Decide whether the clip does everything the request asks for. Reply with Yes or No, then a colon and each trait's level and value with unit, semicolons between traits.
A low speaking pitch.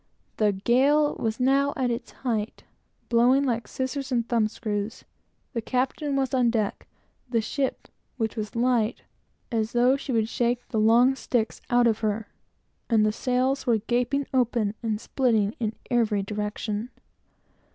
No: high, 235 Hz